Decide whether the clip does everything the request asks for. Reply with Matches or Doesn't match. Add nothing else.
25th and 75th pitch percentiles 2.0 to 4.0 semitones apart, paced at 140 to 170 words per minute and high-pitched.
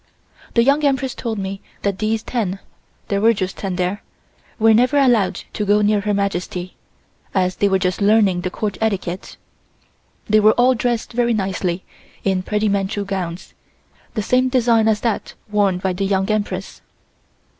Matches